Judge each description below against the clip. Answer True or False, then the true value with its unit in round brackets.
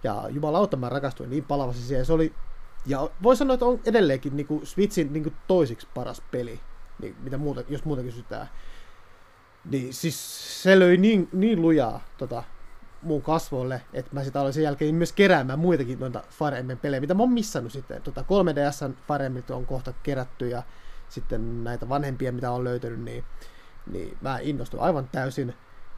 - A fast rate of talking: True (170 wpm)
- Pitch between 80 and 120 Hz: False (140 Hz)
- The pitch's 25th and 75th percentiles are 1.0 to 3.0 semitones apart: False (4.1 semitones)